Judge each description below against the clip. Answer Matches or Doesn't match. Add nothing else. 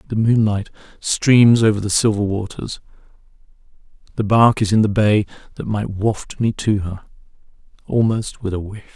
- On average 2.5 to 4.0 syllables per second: Doesn't match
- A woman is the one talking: Doesn't match